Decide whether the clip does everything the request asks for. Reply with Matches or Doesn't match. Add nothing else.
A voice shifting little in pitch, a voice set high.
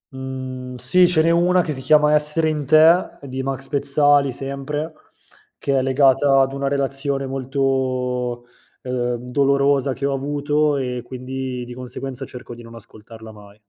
Doesn't match